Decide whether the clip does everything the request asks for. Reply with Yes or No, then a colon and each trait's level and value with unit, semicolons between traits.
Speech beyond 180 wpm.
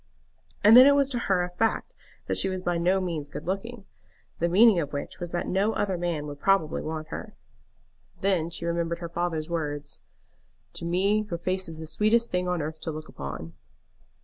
Yes: average, 200 wpm